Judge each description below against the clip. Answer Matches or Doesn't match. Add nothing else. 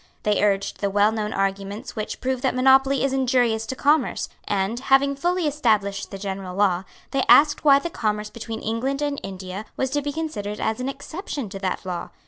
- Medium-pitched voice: Doesn't match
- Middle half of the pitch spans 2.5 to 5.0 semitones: Doesn't match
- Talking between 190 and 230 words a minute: Matches